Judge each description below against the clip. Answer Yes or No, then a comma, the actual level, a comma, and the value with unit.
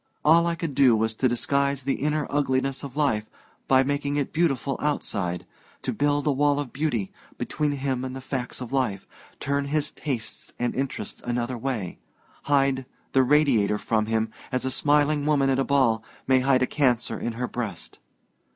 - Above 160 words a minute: Yes, average, 180 wpm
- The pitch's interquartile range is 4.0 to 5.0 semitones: No, average, 2.9 semitones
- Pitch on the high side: No, low, 135 Hz